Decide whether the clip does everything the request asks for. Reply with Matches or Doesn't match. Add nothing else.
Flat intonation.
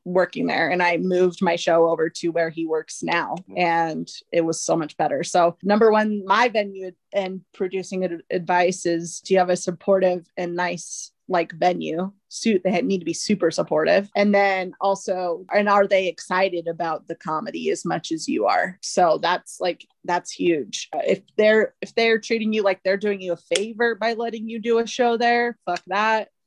Doesn't match